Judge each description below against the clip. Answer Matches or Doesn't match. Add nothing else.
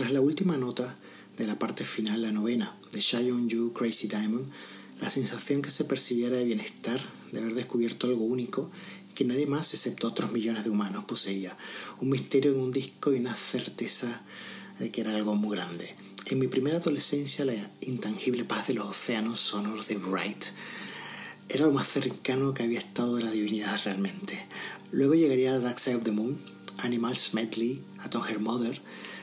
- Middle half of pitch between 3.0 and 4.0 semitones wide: Matches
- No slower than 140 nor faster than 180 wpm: Matches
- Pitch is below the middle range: Matches